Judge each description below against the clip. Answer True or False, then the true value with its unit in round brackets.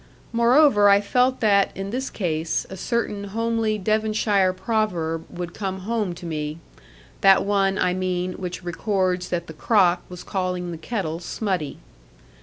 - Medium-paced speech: True (150 wpm)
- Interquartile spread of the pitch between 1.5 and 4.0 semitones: True (3.4 semitones)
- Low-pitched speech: False (190 Hz)